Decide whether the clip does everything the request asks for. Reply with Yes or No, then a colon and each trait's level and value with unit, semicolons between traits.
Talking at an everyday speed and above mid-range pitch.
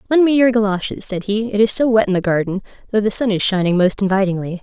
No: fast, 260 wpm; high, 205 Hz